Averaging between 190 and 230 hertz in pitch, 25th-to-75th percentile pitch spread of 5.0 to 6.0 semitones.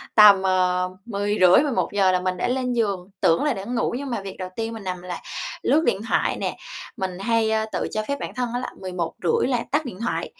No: high, 205 Hz; average, 4.5 semitones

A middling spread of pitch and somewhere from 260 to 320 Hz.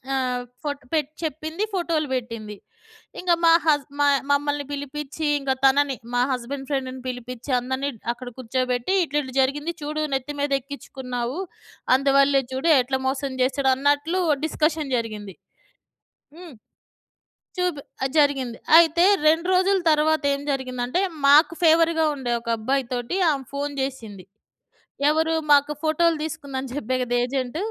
Yes: average, 3.1 semitones; very high, 280 Hz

